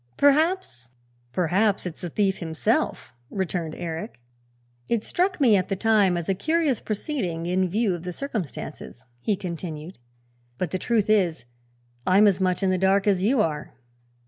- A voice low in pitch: No, high, 190 Hz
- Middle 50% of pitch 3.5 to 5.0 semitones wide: Yes, average, 4.1 semitones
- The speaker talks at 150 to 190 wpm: Yes, average, 165 wpm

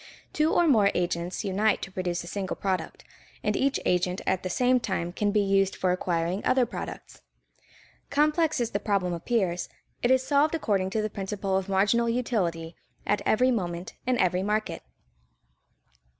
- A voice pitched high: Yes, high, 200 Hz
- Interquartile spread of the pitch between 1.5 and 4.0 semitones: No, average, 4.7 semitones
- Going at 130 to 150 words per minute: No, average, 165 wpm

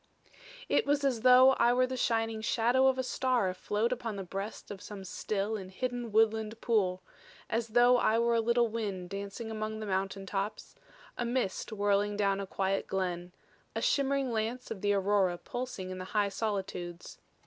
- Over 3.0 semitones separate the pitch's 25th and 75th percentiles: Yes, average, 3.4 semitones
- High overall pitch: Yes, high, 215 Hz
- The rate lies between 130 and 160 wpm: No, average, 180 wpm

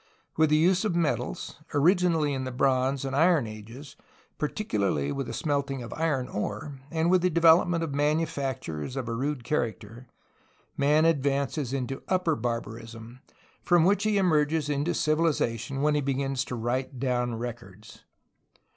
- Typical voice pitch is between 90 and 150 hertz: Yes, medium, 140 Hz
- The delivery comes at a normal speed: Yes, average, 150 wpm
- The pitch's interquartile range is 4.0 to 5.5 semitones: Yes, average, 4.7 semitones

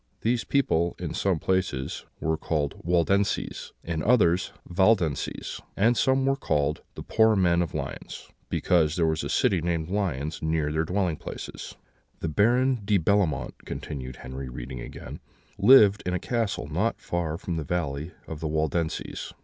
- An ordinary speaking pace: Yes, average, 155 wpm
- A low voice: Yes, very low, 85 Hz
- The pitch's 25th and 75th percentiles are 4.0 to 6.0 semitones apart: Yes, average, 4.6 semitones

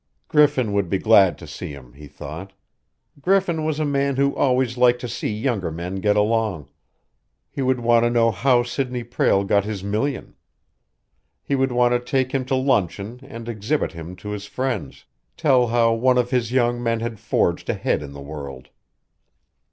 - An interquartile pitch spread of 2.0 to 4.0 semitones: No, average, 4.7 semitones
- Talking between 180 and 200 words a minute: Yes, average, 185 wpm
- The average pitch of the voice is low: Yes, low, 115 Hz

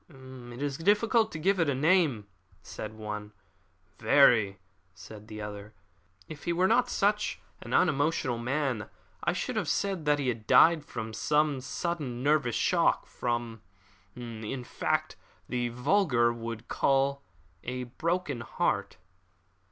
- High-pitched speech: No, low, 130 Hz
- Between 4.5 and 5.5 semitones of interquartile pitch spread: Yes, average, 5.2 semitones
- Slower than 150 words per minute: Yes, average, 140 wpm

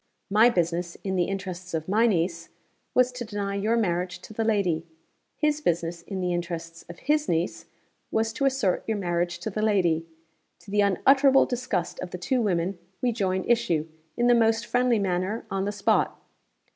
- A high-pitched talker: Yes, high, 195 Hz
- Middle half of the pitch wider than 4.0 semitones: Yes, average, 4.7 semitones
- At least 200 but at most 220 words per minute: No, average, 185 wpm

